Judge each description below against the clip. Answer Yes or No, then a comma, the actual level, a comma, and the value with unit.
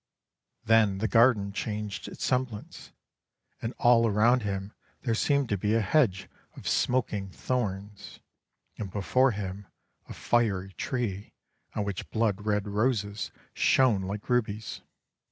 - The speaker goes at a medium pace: No, slow, 130 wpm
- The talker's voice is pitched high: No, low, 105 Hz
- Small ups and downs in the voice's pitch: No, average, 3.0 semitones